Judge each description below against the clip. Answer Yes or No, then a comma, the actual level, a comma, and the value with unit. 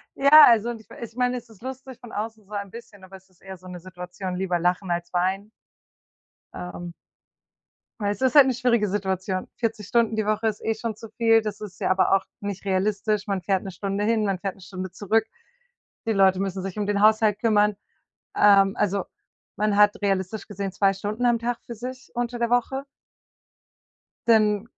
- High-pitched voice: Yes, high, 205 Hz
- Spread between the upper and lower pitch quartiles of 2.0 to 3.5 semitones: Yes, average, 2.9 semitones